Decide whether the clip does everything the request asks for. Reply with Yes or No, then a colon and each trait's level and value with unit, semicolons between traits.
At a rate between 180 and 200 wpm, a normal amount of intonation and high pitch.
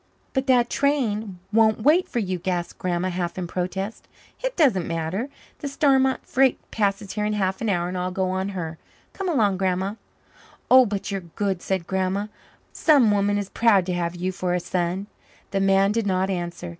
Yes: average, 190 wpm; average, 3.6 semitones; high, 195 Hz